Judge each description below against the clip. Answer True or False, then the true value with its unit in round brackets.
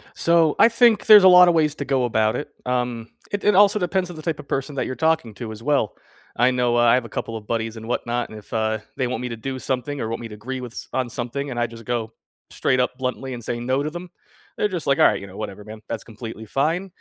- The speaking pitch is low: True (125 Hz)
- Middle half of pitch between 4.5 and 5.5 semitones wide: True (4.9 semitones)